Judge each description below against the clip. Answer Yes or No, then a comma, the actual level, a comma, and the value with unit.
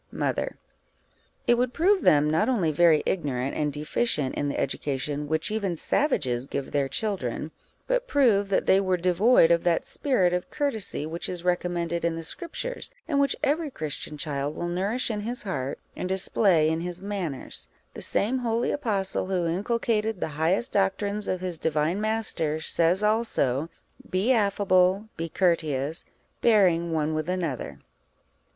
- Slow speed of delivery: No, average, 160 wpm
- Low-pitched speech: No, medium, 180 Hz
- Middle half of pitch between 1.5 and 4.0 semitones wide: No, wide, 5.5 semitones